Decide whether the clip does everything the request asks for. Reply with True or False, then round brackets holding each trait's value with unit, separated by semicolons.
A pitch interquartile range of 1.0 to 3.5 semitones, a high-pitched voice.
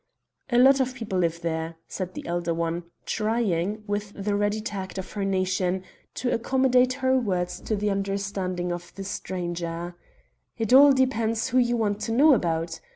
False (4.6 semitones; 200 Hz)